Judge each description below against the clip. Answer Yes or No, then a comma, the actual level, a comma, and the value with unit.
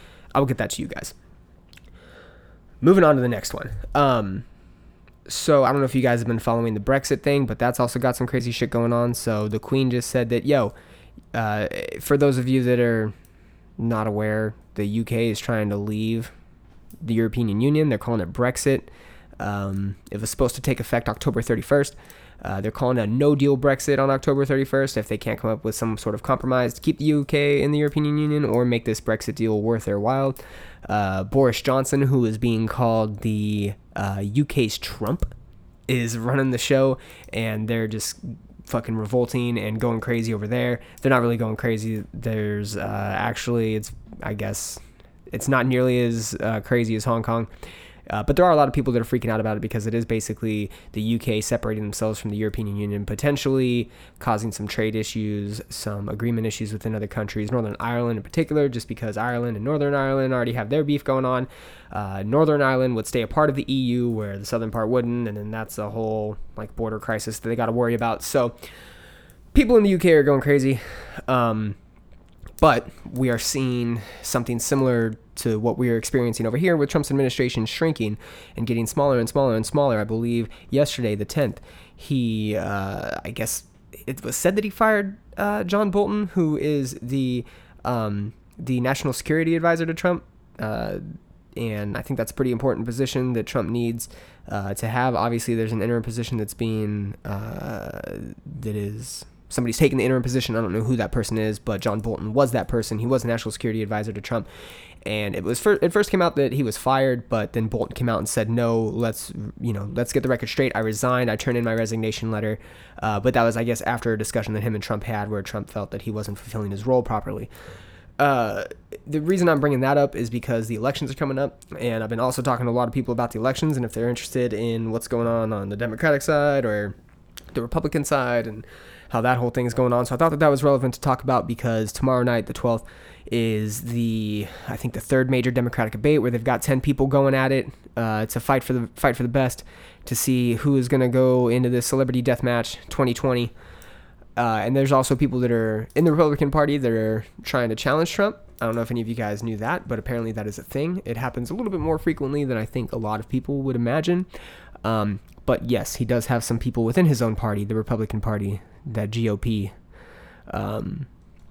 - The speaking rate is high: Yes, fast, 215 wpm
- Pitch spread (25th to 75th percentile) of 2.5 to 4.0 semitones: Yes, average, 3.4 semitones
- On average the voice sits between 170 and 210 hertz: No, low, 120 Hz